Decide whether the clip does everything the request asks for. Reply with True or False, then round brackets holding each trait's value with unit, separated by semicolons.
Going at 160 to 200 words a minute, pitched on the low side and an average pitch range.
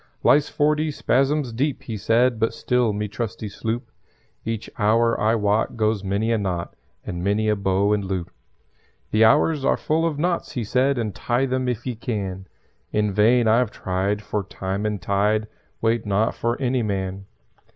True (170 wpm; 110 Hz; 3.5 semitones)